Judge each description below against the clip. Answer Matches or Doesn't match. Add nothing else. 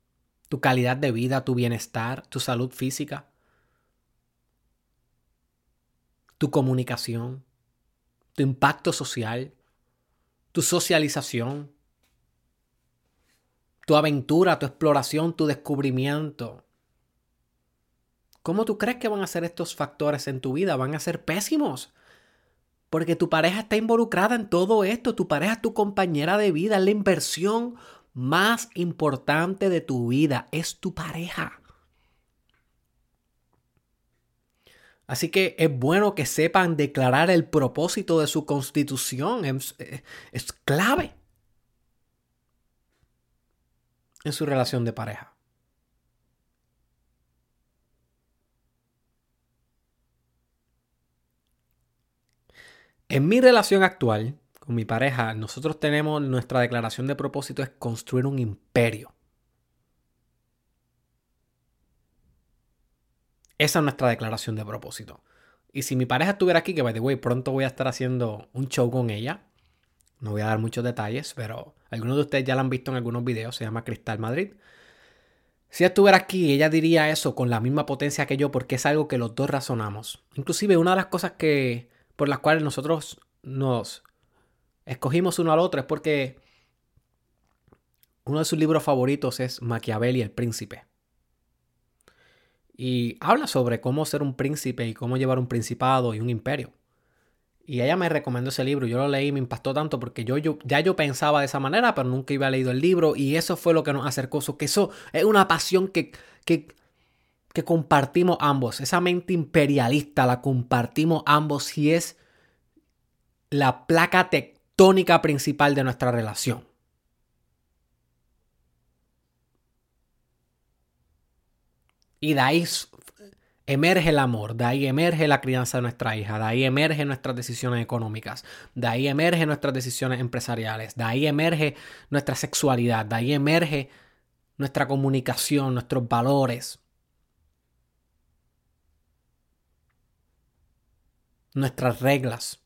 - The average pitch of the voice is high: Doesn't match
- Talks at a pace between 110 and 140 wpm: Matches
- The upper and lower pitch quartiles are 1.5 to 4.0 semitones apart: Doesn't match